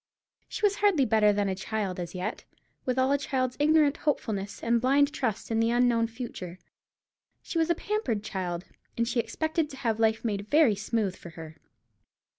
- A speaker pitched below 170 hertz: No, high, 230 Hz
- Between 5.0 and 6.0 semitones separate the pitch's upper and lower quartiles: Yes, wide, 5.6 semitones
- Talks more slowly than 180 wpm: No, average, 185 wpm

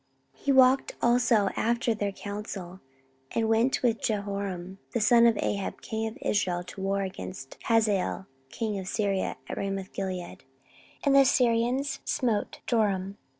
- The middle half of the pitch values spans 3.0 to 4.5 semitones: Yes, average, 3.3 semitones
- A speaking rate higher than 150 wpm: No, average, 145 wpm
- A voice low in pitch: No, high, 210 Hz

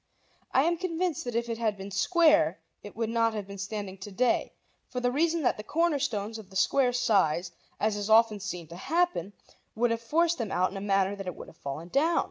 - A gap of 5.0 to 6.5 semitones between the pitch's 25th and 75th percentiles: Yes, wide, 5.6 semitones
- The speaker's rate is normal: No, fast, 235 wpm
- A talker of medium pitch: No, high, 220 Hz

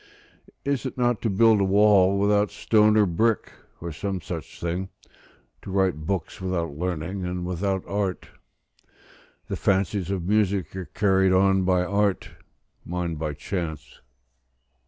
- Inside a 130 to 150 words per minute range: Yes, average, 140 wpm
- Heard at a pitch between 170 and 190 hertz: No, very low, 95 Hz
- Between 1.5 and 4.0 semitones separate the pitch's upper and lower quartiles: Yes, narrow, 2.4 semitones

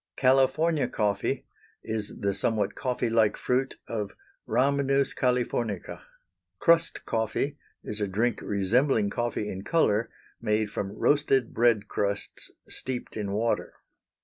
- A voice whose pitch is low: Yes, low, 115 Hz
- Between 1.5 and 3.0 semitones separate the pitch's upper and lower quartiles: No, average, 4.2 semitones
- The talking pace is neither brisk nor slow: No, slow, 120 wpm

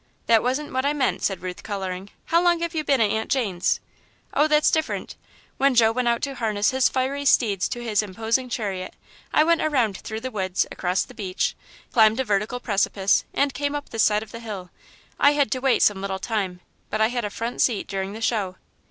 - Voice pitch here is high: Yes, high, 225 Hz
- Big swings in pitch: No, average, 4.8 semitones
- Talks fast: Yes, fast, 220 wpm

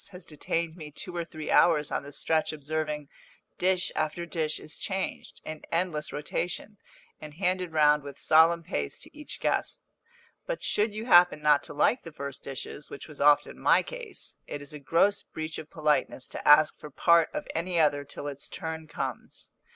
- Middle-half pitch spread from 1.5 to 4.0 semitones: Yes, average, 2.8 semitones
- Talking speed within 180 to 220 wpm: Yes, average, 185 wpm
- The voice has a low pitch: No, medium, 155 Hz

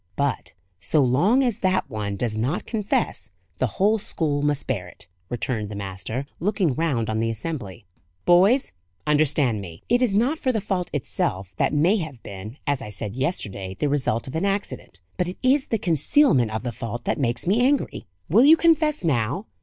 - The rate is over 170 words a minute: Yes, average, 185 wpm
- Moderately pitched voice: Yes, medium, 145 Hz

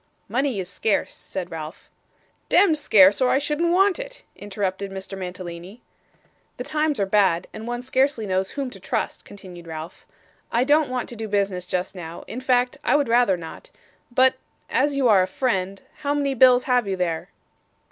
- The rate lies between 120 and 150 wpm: No, average, 180 wpm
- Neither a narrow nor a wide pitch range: No, wide, 5.9 semitones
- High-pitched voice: Yes, high, 220 Hz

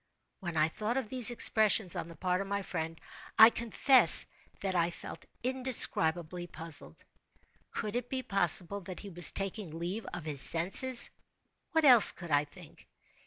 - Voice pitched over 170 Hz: Yes, high, 190 Hz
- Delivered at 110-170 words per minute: Yes, average, 165 wpm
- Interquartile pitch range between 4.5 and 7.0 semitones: Yes, average, 5.3 semitones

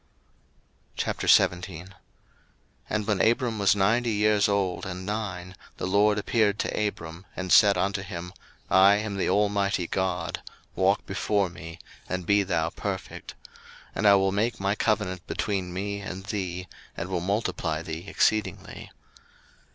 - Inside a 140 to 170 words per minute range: Yes, average, 145 wpm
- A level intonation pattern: Yes, narrow, 2.1 semitones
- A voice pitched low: Yes, very low, 95 Hz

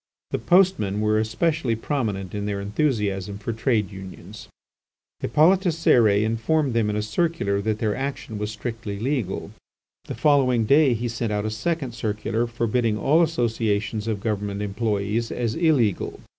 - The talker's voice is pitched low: Yes, low, 110 Hz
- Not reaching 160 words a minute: Yes, average, 150 wpm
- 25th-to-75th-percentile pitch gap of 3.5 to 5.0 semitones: Yes, average, 4.2 semitones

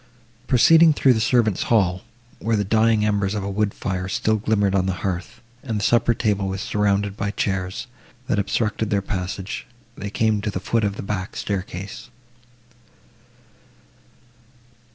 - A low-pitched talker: Yes, low, 105 Hz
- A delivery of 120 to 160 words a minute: Yes, average, 155 wpm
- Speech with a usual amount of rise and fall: No, narrow, 2.3 semitones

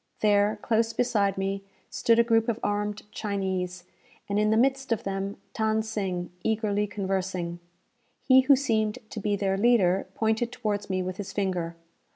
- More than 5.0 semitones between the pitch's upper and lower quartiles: No, narrow, 2.5 semitones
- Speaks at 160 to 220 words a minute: Yes, average, 165 wpm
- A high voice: Yes, high, 205 Hz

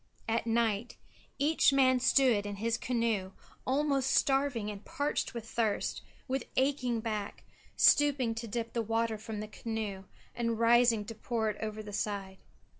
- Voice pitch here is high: Yes, high, 230 Hz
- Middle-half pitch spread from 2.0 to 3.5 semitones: Yes, average, 3.0 semitones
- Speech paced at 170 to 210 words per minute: No, average, 155 wpm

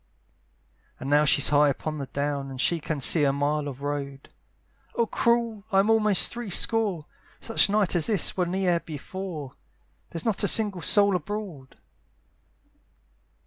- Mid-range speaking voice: Yes, medium, 170 Hz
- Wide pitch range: Yes, wide, 6.1 semitones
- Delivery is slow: No, average, 150 wpm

